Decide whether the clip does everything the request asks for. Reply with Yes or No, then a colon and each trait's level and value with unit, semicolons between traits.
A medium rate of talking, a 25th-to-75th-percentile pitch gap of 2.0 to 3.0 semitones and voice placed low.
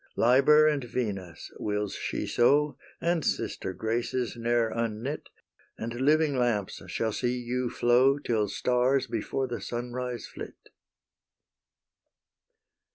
No: slow, 110 wpm; narrow, 2.6 semitones; low, 120 Hz